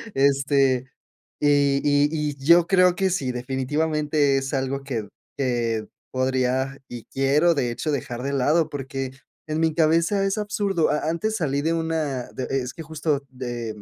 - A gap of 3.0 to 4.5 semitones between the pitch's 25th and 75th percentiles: Yes, average, 3.5 semitones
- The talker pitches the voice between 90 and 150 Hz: Yes, medium, 140 Hz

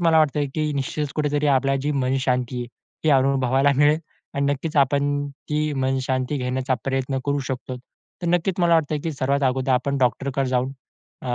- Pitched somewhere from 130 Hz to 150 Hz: Yes, medium, 140 Hz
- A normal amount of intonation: No, narrow, 2.2 semitones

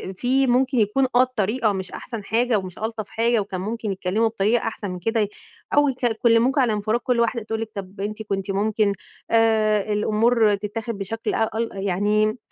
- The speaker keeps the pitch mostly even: Yes, narrow, 2.3 semitones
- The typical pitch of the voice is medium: No, high, 220 Hz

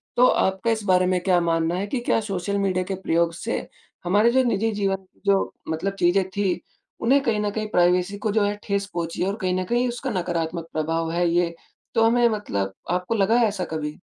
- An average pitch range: Yes, average, 3.4 semitones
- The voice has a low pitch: No, high, 190 Hz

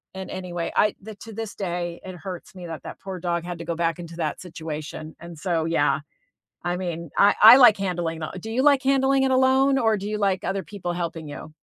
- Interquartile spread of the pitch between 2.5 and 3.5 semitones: No, average, 4.1 semitones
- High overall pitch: No, medium, 180 Hz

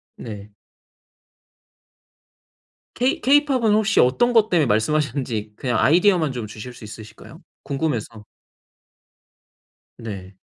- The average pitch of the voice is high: No, low, 130 Hz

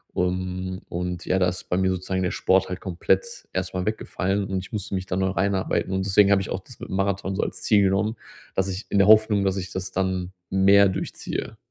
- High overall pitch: No, very low, 95 Hz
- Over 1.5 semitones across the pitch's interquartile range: No, narrow, 1.1 semitones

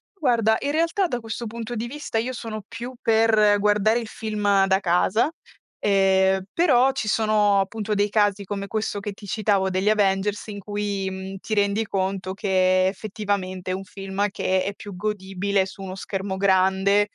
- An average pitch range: No, narrow, 2.3 semitones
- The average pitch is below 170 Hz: No, high, 205 Hz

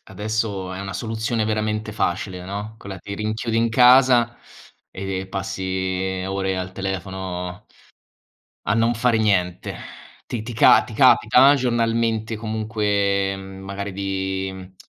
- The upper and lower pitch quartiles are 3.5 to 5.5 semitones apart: No, average, 2.8 semitones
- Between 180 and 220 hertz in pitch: No, low, 100 Hz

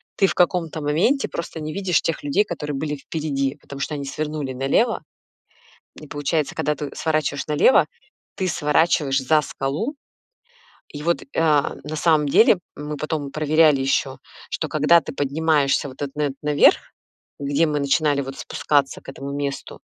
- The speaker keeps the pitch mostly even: Yes, narrow, 2.2 semitones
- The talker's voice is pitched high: No, medium, 150 Hz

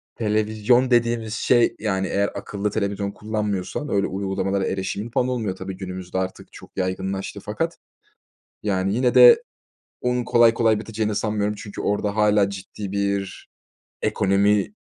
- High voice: No, low, 105 Hz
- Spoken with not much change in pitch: Yes, narrow, 2.2 semitones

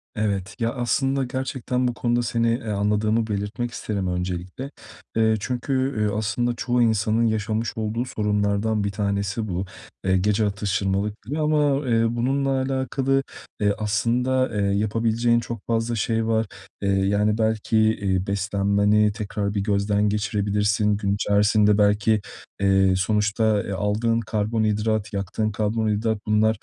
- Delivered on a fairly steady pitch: Yes, narrow, 2.2 semitones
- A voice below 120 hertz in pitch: Yes, low, 105 Hz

